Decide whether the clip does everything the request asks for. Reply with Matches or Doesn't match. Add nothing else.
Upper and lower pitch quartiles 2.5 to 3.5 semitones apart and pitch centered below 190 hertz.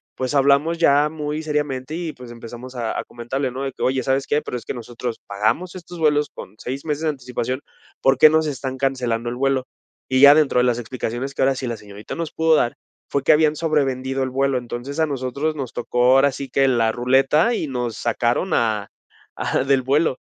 Matches